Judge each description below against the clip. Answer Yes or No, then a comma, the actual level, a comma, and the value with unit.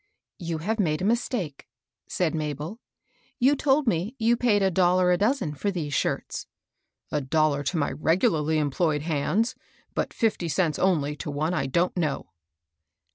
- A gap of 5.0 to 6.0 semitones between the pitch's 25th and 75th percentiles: Yes, average, 5.3 semitones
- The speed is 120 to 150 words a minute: No, average, 170 wpm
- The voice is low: No, medium, 170 Hz